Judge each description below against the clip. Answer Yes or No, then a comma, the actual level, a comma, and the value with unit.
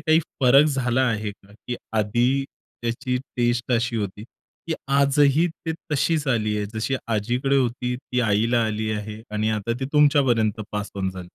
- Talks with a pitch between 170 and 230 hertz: No, low, 120 Hz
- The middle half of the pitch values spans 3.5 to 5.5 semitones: Yes, average, 4.0 semitones